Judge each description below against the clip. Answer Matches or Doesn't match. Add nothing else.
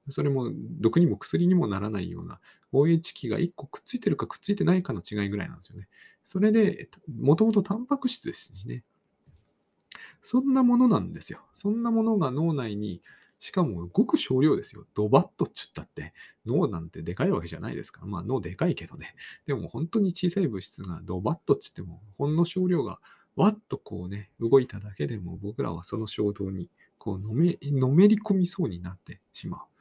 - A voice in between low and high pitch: Matches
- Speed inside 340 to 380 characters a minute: Doesn't match